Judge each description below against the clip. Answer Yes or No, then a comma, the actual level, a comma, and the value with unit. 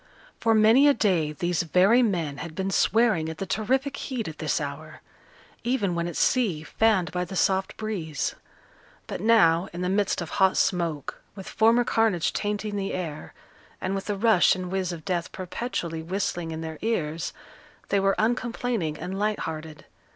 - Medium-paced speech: Yes, average, 175 wpm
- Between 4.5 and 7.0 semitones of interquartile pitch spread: Yes, average, 4.9 semitones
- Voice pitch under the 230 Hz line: Yes, high, 190 Hz